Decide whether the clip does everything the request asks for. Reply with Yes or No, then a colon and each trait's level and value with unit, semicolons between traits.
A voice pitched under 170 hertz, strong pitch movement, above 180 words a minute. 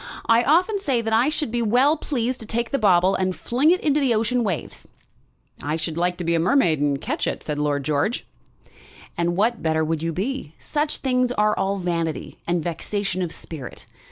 No: high, 205 Hz; wide, 7.2 semitones; fast, 205 wpm